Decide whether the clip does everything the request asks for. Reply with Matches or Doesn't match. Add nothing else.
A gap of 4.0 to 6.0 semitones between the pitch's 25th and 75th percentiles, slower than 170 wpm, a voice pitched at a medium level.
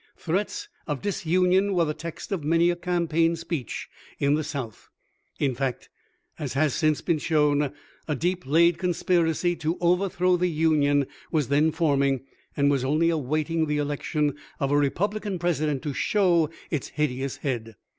Doesn't match